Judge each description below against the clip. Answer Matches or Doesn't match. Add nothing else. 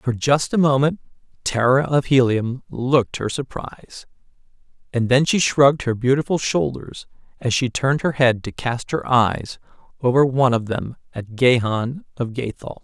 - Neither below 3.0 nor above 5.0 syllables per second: Matches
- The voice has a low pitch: Matches